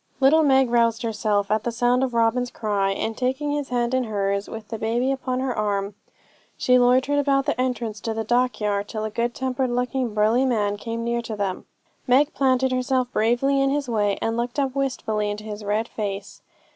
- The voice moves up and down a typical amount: Yes, average, 3.3 semitones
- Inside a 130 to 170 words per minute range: No, average, 200 wpm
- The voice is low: No, high, 235 Hz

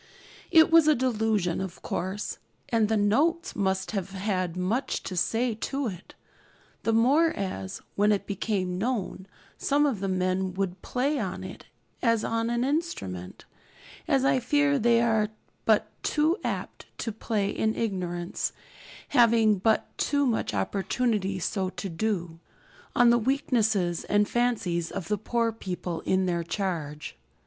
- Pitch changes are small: No, average, 4.3 semitones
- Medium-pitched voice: No, high, 210 Hz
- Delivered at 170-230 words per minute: No, average, 150 wpm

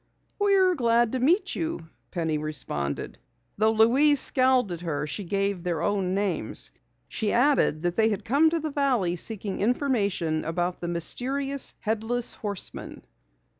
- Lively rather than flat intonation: Yes, wide, 6.9 semitones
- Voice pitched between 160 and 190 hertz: No, high, 220 Hz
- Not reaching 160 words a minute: Yes, average, 145 wpm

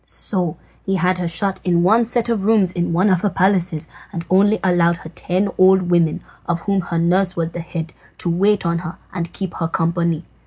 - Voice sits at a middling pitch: Yes, medium, 180 Hz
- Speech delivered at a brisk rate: Yes, fast, 210 wpm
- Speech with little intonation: Yes, narrow, 2.3 semitones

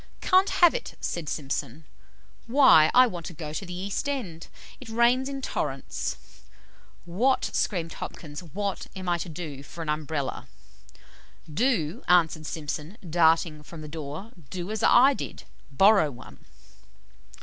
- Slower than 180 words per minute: Yes, average, 145 wpm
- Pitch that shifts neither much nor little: No, wide, 6.4 semitones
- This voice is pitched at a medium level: Yes, medium, 175 Hz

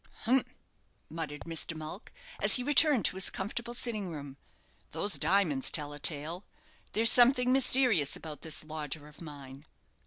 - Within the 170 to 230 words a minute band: No, average, 150 wpm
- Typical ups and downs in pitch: No, wide, 8.0 semitones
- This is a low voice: No, medium, 165 Hz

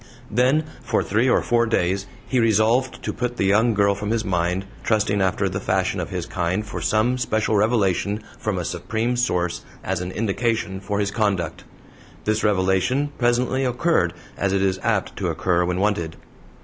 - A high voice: No, low, 105 Hz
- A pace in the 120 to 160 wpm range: No, average, 175 wpm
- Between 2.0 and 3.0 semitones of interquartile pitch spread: No, average, 3.8 semitones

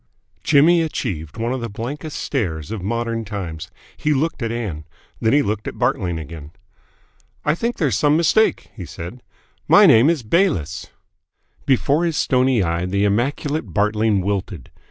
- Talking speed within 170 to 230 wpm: No, average, 155 wpm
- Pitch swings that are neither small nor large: No, wide, 7.3 semitones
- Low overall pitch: Yes, low, 115 Hz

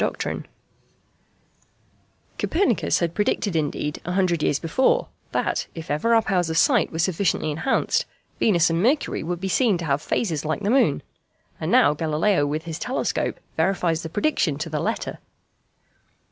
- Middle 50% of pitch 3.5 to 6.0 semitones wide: Yes, average, 4.4 semitones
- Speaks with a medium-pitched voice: Yes, medium, 170 Hz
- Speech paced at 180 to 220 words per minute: No, average, 160 wpm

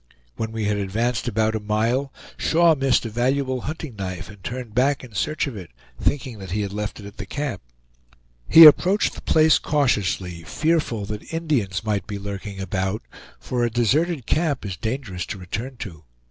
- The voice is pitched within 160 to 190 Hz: No, low, 115 Hz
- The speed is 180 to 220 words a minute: Yes, average, 185 wpm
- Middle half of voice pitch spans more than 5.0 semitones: Yes, wide, 5.4 semitones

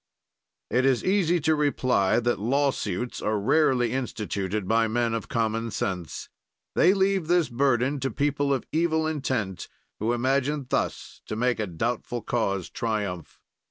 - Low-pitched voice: Yes, low, 120 Hz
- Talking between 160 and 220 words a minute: No, average, 145 wpm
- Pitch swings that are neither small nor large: Yes, average, 4.8 semitones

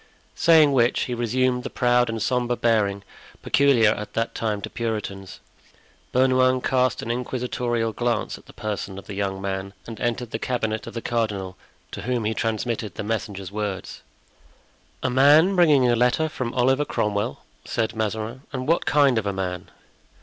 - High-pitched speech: No, low, 115 Hz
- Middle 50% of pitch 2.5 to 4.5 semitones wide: Yes, average, 3.2 semitones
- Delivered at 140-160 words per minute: No, average, 170 wpm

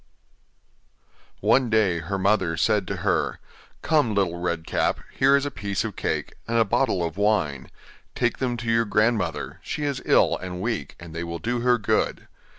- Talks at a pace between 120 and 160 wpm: No, average, 180 wpm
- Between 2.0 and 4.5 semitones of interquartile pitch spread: No, average, 5.3 semitones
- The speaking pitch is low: Yes, low, 105 Hz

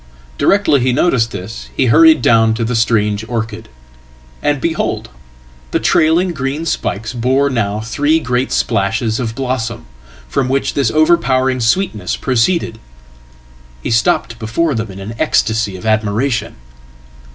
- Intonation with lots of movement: No, average, 3.9 semitones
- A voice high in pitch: No, low, 120 Hz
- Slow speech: Yes, slow, 125 wpm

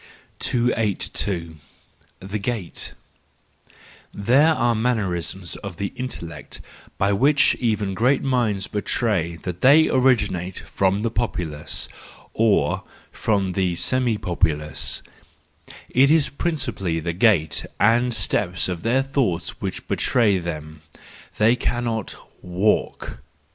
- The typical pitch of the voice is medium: No, low, 105 Hz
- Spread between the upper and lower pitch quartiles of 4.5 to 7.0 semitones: Yes, average, 5.3 semitones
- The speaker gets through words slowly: Yes, slow, 105 wpm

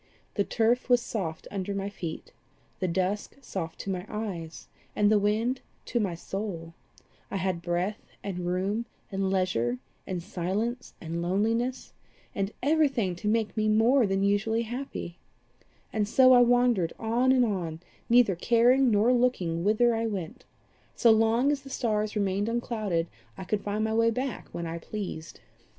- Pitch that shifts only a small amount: No, average, 4.1 semitones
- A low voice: No, high, 210 Hz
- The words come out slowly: No, average, 160 wpm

